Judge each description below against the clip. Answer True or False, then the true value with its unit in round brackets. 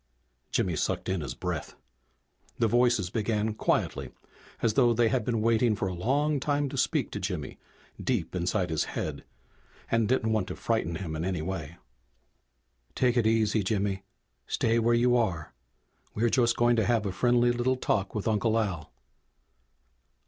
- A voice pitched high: False (110 Hz)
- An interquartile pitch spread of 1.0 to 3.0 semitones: False (4.0 semitones)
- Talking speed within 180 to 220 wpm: False (165 wpm)